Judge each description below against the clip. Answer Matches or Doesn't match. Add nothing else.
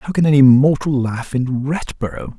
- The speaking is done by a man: Matches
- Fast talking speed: Doesn't match